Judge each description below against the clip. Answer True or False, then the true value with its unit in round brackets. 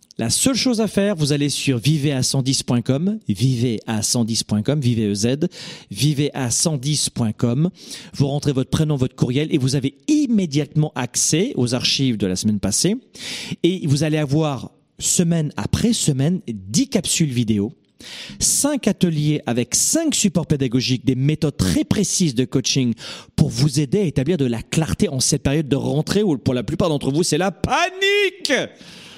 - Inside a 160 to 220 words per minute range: False (150 wpm)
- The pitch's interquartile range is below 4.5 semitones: False (5.4 semitones)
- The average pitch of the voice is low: False (150 Hz)